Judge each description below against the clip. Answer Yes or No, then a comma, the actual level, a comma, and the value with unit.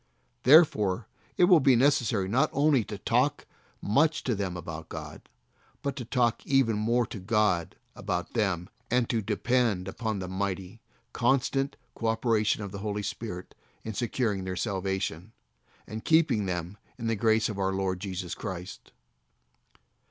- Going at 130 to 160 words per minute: Yes, average, 150 wpm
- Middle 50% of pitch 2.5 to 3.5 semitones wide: No, average, 4.3 semitones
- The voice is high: No, low, 110 Hz